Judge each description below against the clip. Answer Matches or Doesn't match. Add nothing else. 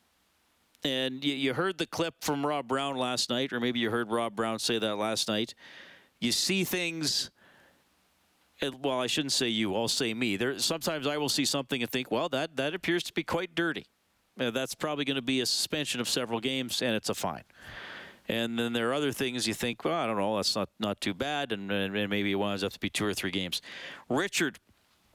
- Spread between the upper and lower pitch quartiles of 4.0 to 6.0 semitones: Matches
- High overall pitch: Doesn't match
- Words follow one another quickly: Matches